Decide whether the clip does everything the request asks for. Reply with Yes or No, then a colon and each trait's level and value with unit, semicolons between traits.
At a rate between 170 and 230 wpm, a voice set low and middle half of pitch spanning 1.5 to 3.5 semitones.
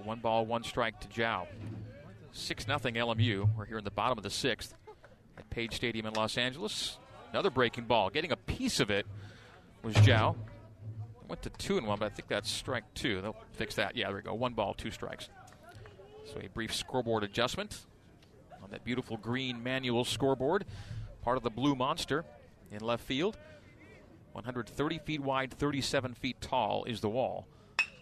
Yes: average, 180 wpm; low, 115 Hz; average, 2.8 semitones